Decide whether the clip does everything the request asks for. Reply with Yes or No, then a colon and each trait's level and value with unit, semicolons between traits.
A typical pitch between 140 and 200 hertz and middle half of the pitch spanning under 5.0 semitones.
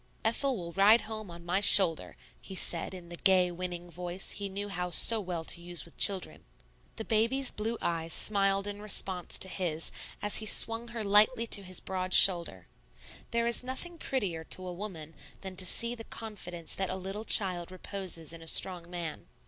Yes: high, 190 Hz; average, 3.5 semitones